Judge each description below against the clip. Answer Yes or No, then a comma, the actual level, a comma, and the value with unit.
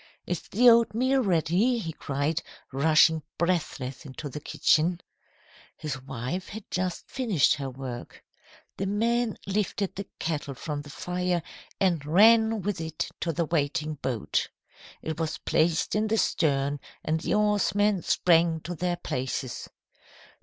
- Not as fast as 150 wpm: Yes, average, 140 wpm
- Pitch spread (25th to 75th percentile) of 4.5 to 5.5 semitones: Yes, average, 5.2 semitones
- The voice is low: No, medium, 170 Hz